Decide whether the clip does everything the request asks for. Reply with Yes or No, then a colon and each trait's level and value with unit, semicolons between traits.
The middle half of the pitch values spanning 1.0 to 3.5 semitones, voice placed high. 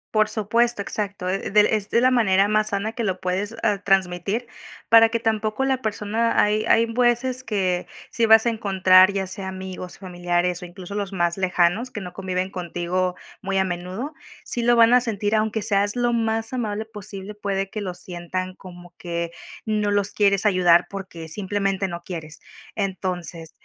Yes: average, 3.1 semitones; high, 200 Hz